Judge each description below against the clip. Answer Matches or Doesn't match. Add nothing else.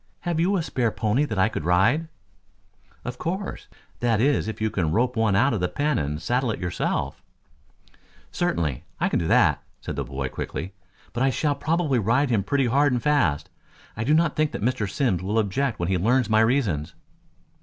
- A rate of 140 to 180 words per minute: Doesn't match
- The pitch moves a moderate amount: Doesn't match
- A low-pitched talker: Matches